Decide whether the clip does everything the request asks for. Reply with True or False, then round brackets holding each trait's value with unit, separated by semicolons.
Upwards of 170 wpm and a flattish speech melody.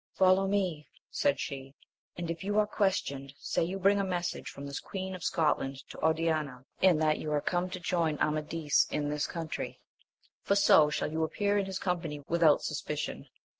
False (190 wpm; 4.0 semitones)